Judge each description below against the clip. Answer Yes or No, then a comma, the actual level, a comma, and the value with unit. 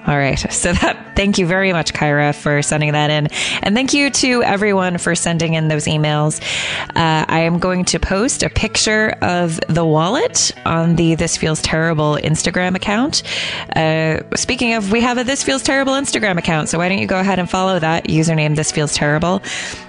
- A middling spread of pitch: Yes, average, 4.0 semitones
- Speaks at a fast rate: No, average, 195 wpm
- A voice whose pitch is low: No, medium, 170 Hz